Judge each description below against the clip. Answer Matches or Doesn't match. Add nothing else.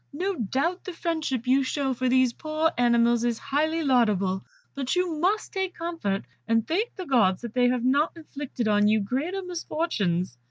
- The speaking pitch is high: Matches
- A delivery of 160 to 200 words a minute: Matches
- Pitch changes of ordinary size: Doesn't match